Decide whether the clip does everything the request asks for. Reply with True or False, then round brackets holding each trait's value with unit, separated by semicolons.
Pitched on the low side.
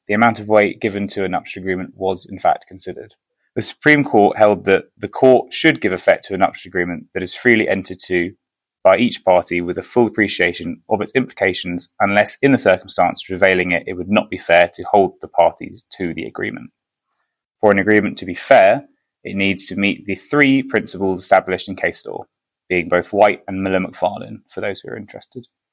True (95 Hz)